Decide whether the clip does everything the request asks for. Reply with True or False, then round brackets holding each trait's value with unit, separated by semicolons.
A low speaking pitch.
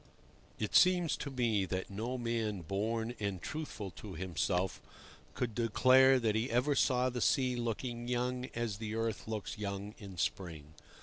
True (115 Hz)